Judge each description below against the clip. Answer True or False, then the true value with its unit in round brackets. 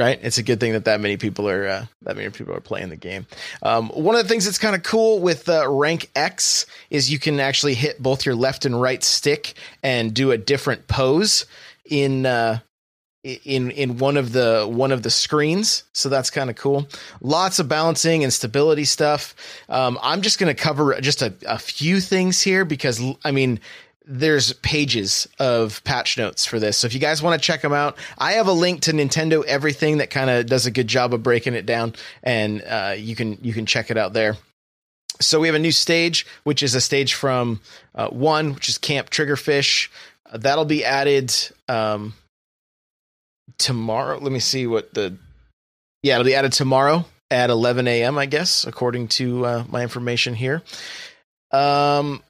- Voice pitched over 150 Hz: False (135 Hz)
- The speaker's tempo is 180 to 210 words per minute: True (200 wpm)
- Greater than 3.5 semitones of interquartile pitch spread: True (3.9 semitones)